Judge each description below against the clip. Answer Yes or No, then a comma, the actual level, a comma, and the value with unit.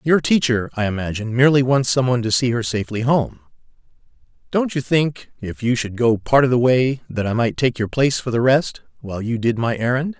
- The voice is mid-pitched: No, low, 125 Hz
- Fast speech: Yes, fast, 225 wpm